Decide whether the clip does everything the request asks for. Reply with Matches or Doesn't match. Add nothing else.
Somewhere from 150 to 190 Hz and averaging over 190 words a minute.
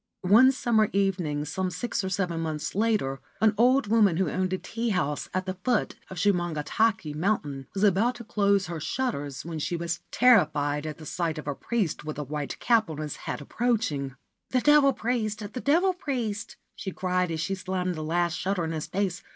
Matches